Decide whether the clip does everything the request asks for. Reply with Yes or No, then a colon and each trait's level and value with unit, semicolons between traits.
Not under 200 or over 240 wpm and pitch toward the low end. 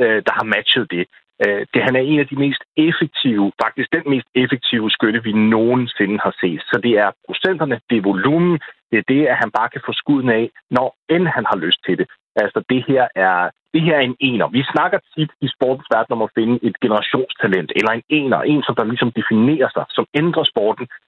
Yes: average, 220 wpm; low, 125 Hz